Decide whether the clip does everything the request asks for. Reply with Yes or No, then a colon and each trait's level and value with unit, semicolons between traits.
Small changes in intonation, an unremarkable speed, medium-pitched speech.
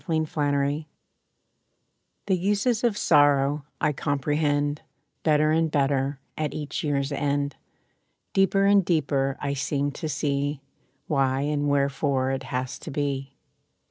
No: narrow, 1.8 semitones; slow, 125 wpm; medium, 145 Hz